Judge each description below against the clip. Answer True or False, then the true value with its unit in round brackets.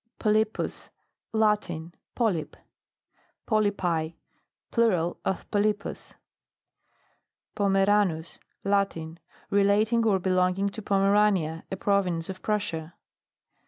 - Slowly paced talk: True (85 wpm)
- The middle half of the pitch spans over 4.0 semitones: False (3.2 semitones)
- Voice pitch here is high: True (195 Hz)